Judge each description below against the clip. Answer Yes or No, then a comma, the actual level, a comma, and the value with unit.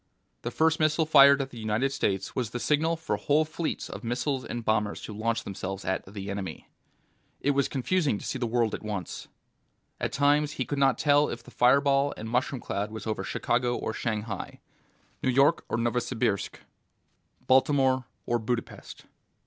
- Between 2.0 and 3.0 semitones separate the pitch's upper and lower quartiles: No, average, 4.4 semitones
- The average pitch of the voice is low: Yes, low, 125 Hz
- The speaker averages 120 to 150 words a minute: No, average, 175 wpm